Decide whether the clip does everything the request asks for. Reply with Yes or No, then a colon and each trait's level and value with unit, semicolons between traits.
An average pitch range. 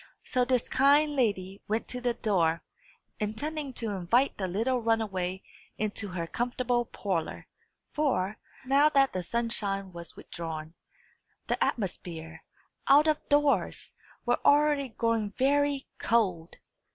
No: wide, 6.3 semitones